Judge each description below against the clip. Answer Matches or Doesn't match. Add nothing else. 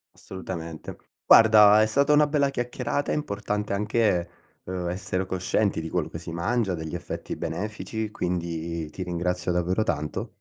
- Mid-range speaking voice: Doesn't match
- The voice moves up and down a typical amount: Matches